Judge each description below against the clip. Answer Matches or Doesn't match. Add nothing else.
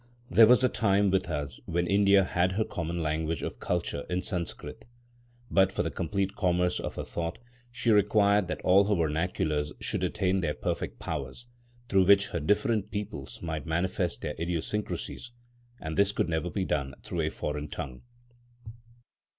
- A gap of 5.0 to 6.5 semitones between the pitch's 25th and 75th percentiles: Doesn't match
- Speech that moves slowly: Doesn't match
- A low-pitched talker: Matches